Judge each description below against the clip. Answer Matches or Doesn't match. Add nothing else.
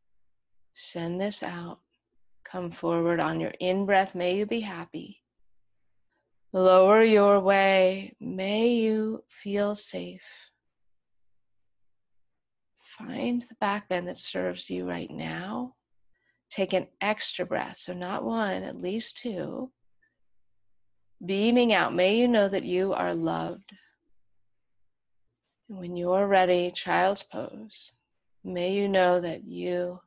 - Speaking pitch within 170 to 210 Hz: Matches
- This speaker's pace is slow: Matches